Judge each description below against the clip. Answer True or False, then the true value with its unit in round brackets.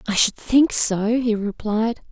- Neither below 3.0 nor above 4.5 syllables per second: True (3.8 syllables/s)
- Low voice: False (225 Hz)